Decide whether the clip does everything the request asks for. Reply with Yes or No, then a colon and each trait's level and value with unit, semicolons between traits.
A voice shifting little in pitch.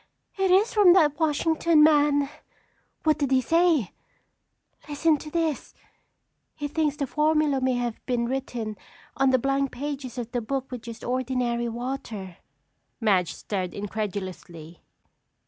No: average, 4.3 semitones